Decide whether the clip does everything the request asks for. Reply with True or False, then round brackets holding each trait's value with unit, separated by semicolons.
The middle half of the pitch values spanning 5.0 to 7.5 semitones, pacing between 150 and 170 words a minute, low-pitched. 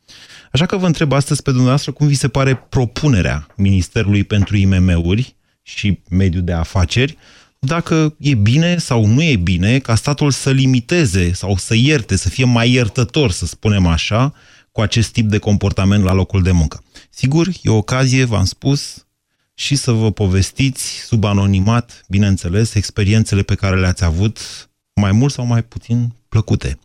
True (5.3 semitones; 165 wpm; 110 Hz)